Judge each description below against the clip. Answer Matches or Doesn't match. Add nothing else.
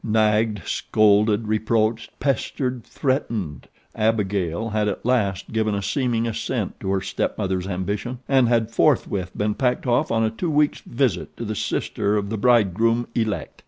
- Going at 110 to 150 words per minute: Doesn't match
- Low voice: Matches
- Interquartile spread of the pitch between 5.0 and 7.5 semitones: Doesn't match